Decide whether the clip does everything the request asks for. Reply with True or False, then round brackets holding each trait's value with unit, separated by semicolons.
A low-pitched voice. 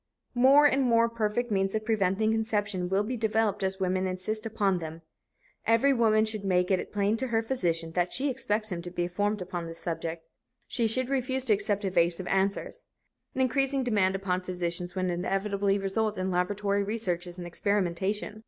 False (200 Hz)